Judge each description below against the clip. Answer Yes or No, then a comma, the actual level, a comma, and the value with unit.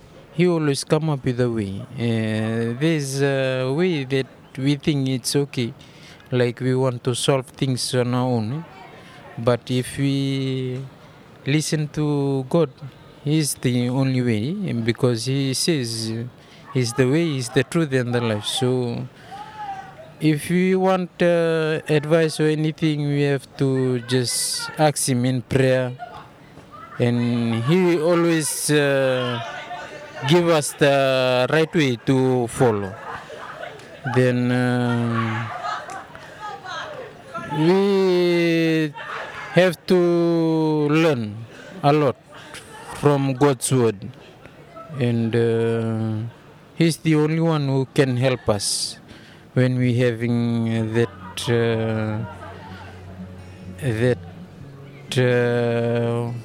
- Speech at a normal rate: No, slow, 110 wpm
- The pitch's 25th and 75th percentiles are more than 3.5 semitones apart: Yes, average, 4.4 semitones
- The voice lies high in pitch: No, low, 135 Hz